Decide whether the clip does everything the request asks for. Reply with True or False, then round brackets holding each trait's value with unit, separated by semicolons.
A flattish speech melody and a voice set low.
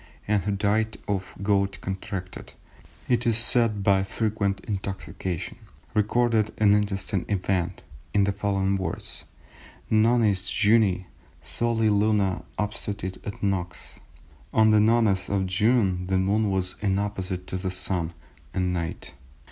True (2.3 semitones; 100 Hz)